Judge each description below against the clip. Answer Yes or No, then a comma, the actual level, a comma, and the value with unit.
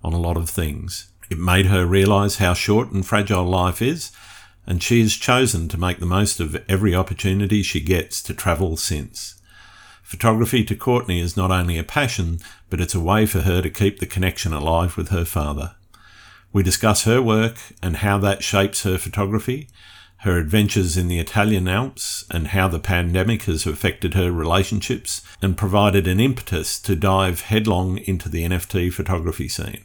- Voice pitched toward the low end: Yes, very low, 95 Hz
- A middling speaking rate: Yes, average, 175 wpm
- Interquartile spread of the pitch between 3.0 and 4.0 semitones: No, narrow, 2.5 semitones